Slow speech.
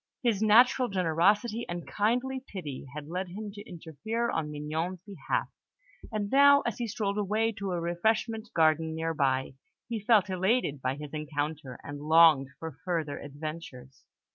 No: average, 155 wpm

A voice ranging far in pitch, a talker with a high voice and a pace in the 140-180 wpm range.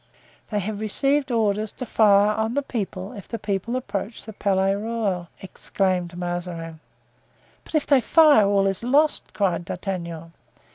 No: average, 3.8 semitones; high, 205 Hz; average, 150 wpm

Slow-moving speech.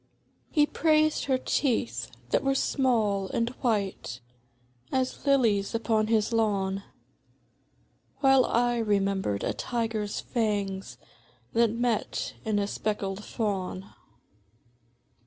Yes: slow, 100 wpm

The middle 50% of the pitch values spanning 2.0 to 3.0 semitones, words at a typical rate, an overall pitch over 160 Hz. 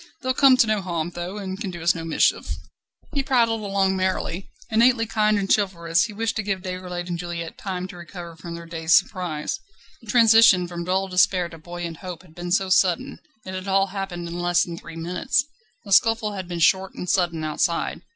No: average, 2.7 semitones; fast, 210 wpm; medium, 185 Hz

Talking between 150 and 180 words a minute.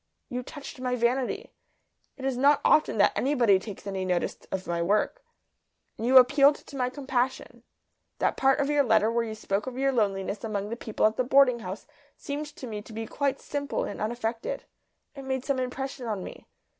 No: average, 195 wpm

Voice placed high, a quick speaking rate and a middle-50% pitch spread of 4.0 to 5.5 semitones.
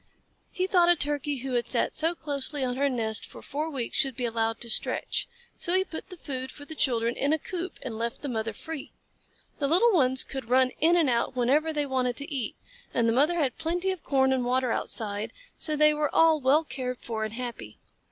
Yes: very high, 270 Hz; fast, 225 wpm; average, 4.3 semitones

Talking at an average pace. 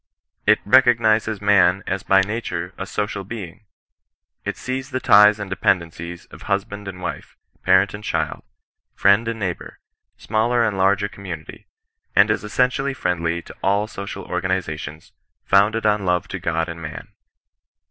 Yes: average, 150 wpm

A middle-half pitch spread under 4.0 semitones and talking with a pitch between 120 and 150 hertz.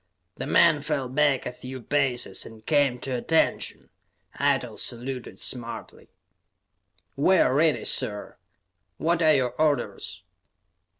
Yes: average, 3.3 semitones; low, 135 Hz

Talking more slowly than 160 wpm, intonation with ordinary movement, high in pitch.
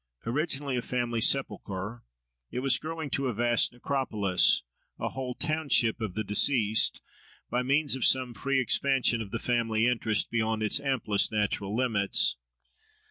No: average, 145 wpm; average, 3.4 semitones; low, 120 Hz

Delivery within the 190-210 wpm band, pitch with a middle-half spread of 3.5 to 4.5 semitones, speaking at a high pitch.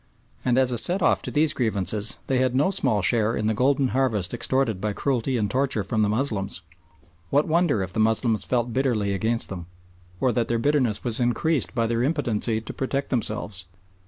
No: average, 195 wpm; average, 3.8 semitones; low, 120 Hz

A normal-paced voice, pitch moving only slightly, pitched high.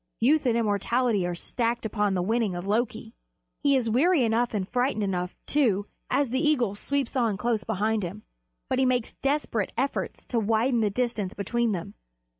No: average, 180 wpm; average, 3.6 semitones; high, 230 Hz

